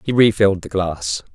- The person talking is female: No, male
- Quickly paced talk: No, average, 180 wpm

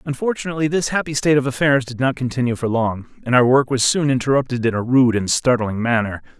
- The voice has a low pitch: Yes, low, 130 Hz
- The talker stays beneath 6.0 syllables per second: No, 6.4 syllables/s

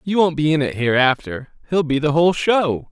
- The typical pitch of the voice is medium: Yes, medium, 150 Hz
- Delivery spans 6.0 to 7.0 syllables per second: No, 5.3 syllables/s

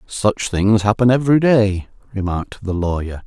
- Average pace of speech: Yes, average, 145 wpm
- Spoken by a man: Yes, male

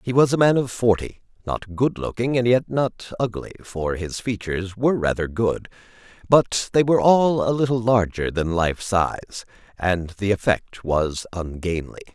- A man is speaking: Yes, male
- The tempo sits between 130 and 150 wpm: No, average, 165 wpm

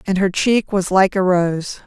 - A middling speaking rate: No, fast, 225 wpm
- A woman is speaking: Yes, female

